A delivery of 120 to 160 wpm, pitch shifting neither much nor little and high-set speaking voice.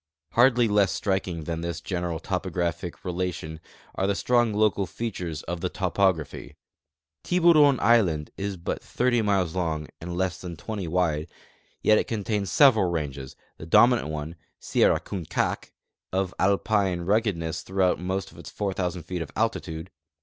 No: average, 145 wpm; average, 3.7 semitones; very low, 95 Hz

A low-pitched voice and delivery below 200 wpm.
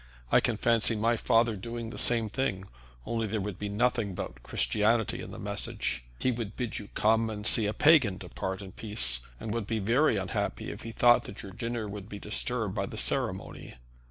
No: low, 110 Hz; fast, 205 wpm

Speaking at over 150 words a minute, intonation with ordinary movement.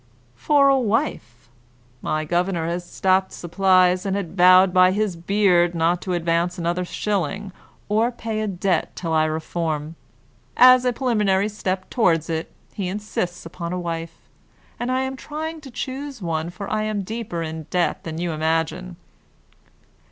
Yes: average, 160 wpm; average, 4.0 semitones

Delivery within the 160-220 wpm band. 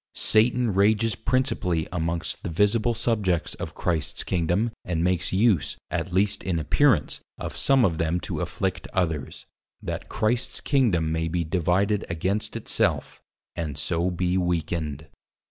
No: average, 145 wpm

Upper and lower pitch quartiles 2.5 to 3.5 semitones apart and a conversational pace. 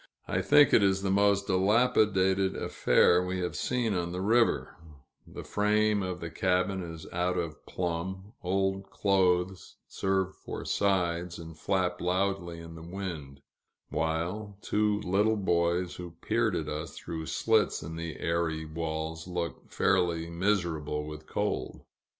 Yes: average, 2.8 semitones; average, 145 wpm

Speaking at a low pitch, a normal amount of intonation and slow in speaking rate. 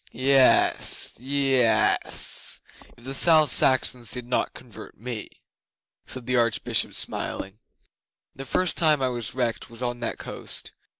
No: low, 125 Hz; narrow, 2.3 semitones; slow, 130 wpm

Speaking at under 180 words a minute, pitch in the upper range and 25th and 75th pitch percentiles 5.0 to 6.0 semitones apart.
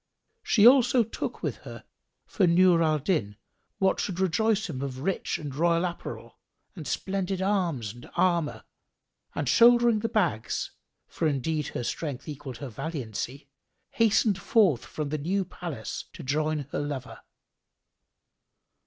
No: average, 140 wpm; medium, 165 Hz; wide, 5.6 semitones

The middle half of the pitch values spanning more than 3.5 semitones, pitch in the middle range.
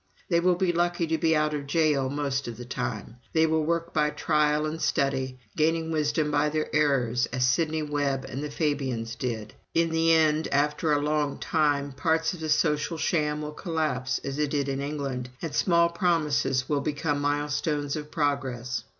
No: narrow, 2.4 semitones; medium, 150 Hz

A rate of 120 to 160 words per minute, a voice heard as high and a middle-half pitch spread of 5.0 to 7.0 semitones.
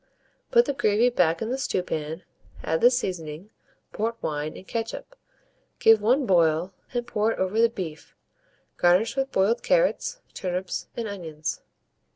Yes: average, 155 wpm; high, 205 Hz; wide, 5.6 semitones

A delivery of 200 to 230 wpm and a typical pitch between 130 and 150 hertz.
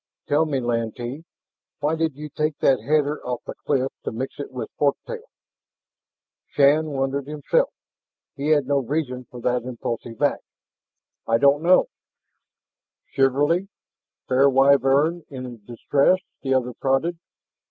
No: average, 140 wpm; medium, 140 Hz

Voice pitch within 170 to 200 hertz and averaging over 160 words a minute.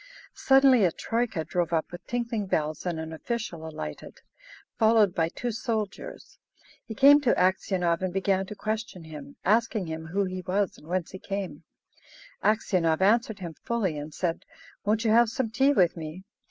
Yes: high, 190 Hz; average, 170 wpm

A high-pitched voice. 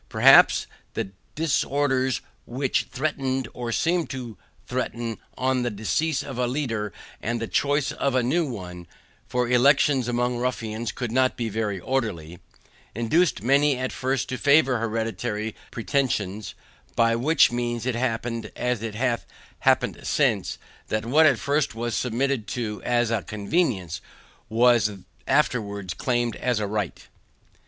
No: low, 120 Hz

